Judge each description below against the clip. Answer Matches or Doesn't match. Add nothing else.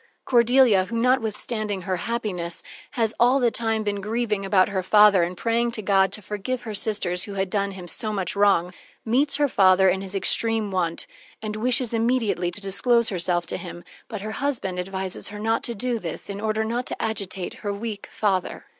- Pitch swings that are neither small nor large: Matches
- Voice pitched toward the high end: Matches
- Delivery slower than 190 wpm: Doesn't match